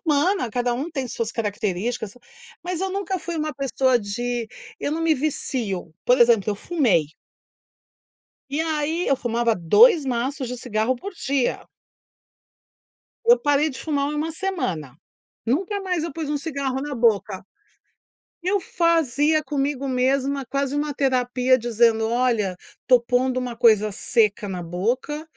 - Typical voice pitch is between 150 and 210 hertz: No, very high, 260 Hz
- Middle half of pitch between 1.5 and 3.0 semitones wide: No, average, 4.6 semitones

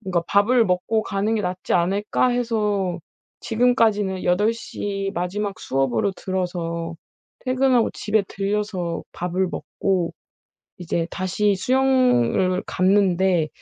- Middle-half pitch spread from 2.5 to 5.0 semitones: Yes, average, 3.2 semitones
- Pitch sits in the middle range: No, high, 195 Hz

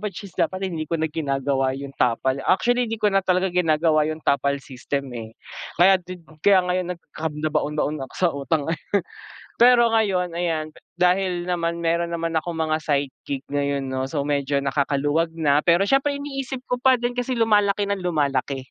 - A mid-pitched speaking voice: Yes, medium, 165 Hz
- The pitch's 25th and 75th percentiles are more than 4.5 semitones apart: Yes, average, 5.1 semitones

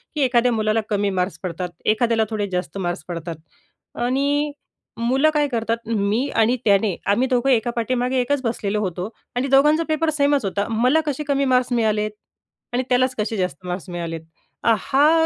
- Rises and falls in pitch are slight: No, average, 4.7 semitones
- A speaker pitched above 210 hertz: Yes, high, 230 Hz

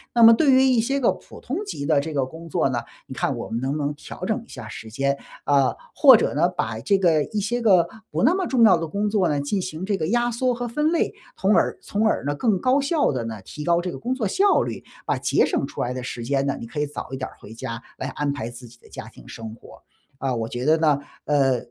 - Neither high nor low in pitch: Yes, medium, 155 Hz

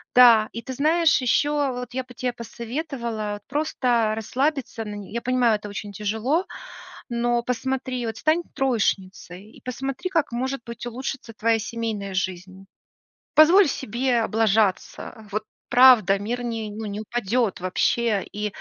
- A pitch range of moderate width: Yes, average, 3.3 semitones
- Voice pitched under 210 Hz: No, high, 235 Hz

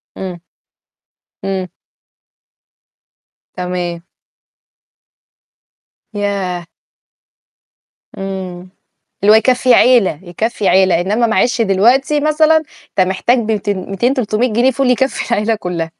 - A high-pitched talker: Yes, high, 205 Hz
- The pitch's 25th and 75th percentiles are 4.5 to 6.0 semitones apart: Yes, average, 4.9 semitones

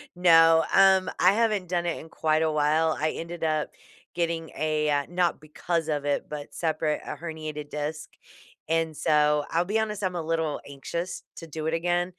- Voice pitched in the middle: Yes, medium, 160 Hz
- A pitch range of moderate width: No, narrow, 2.2 semitones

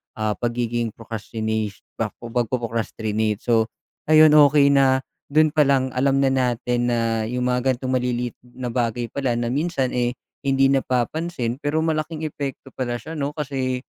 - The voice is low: Yes, low, 125 Hz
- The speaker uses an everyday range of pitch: Yes, average, 3.0 semitones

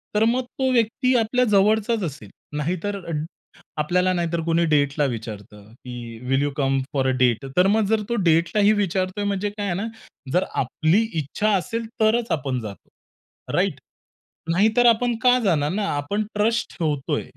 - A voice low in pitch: No, medium, 185 Hz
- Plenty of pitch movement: Yes, wide, 7.0 semitones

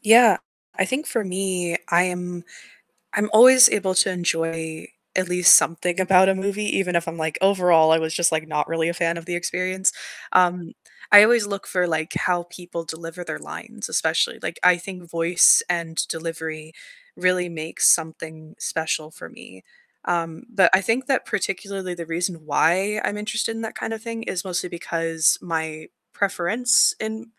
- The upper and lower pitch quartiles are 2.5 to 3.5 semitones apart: Yes, average, 2.9 semitones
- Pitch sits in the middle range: Yes, medium, 180 Hz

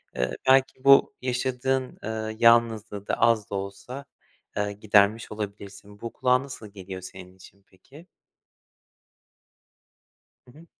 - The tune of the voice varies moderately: Yes, average, 4.1 semitones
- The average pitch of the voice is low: Yes, low, 110 Hz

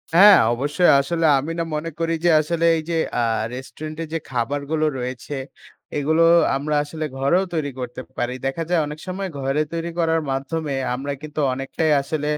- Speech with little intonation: No, average, 3.2 semitones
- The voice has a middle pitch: Yes, medium, 150 Hz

